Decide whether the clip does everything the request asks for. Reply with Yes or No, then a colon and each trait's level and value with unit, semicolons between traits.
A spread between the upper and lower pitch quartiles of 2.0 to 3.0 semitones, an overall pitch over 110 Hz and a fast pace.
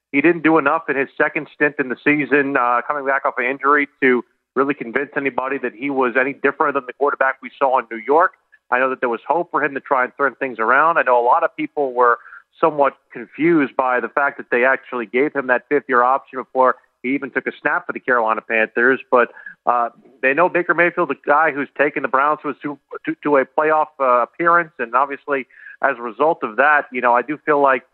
Yes: average, 2.7 semitones; medium, 140 Hz; fast, 245 wpm